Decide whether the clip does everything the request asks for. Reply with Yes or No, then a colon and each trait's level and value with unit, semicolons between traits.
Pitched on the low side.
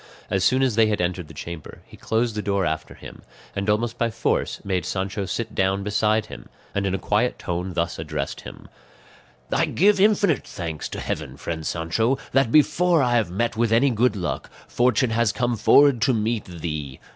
Yes: low, 105 Hz